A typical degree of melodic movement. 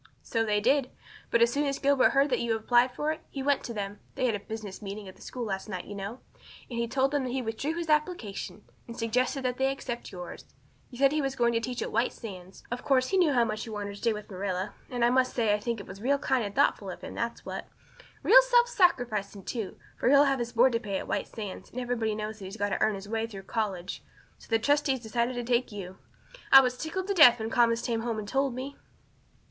Yes: average, 4.0 semitones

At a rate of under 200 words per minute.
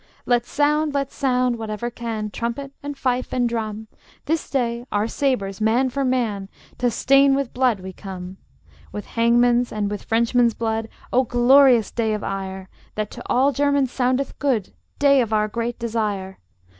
Yes: average, 165 wpm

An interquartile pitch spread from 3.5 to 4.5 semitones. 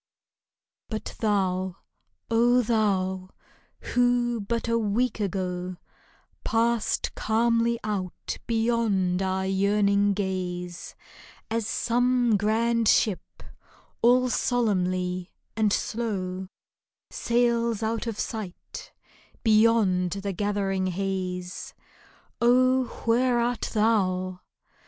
Yes: average, 3.8 semitones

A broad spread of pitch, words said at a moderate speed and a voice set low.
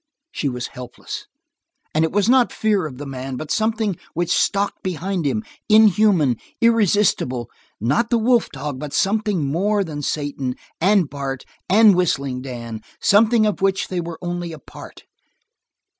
No: wide, 7.0 semitones; average, 160 wpm; medium, 175 Hz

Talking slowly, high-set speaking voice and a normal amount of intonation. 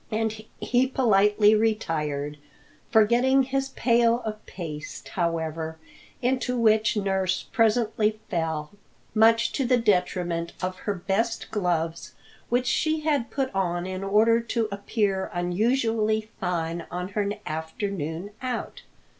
Yes: slow, 120 wpm; high, 210 Hz; average, 4.8 semitones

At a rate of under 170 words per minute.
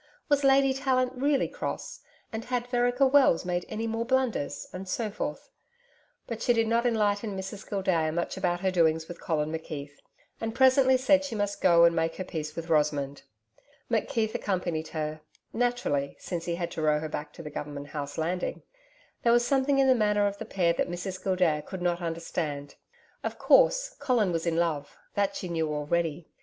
No: average, 190 wpm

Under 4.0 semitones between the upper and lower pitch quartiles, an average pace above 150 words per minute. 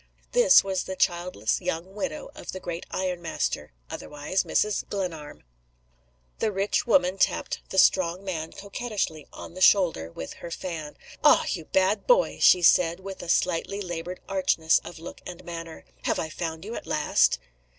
Yes: average, 3.0 semitones; average, 160 wpm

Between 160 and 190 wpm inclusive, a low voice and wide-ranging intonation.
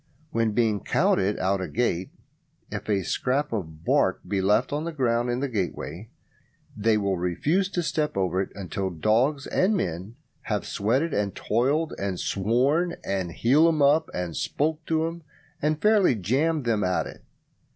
Yes: average, 170 wpm; low, 115 Hz; wide, 7.6 semitones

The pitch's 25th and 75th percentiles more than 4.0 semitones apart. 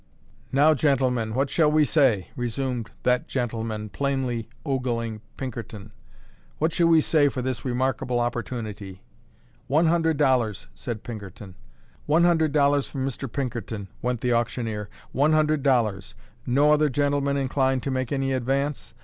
No: average, 3.6 semitones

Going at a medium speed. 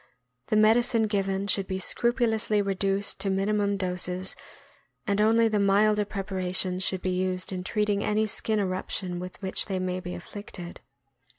Yes: average, 160 wpm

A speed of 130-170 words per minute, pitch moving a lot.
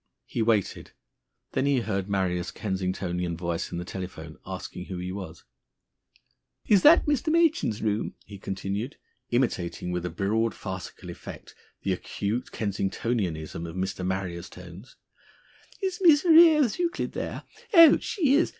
Yes: average, 140 wpm; wide, 7.1 semitones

